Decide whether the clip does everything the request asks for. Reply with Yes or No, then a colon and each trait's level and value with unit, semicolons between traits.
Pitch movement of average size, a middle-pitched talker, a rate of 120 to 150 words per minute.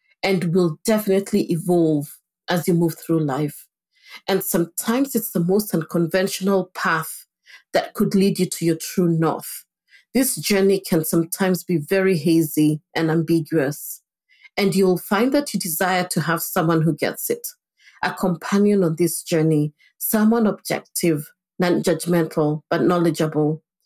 Yes: average, 3.1 semitones; medium, 180 Hz; average, 140 wpm